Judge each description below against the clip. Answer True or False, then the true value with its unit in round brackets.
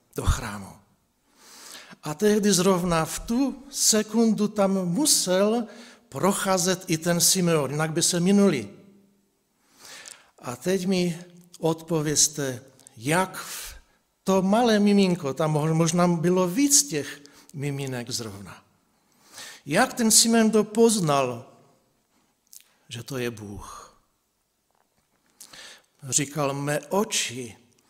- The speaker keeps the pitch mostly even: False (6.8 semitones)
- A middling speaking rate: False (100 wpm)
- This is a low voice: False (175 Hz)